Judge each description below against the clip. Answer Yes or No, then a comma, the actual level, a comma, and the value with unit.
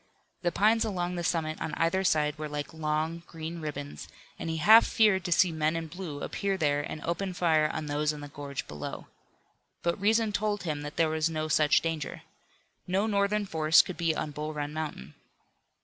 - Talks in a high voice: No, medium, 160 Hz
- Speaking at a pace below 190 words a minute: No, average, 195 wpm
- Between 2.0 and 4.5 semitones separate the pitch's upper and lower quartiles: Yes, average, 3.2 semitones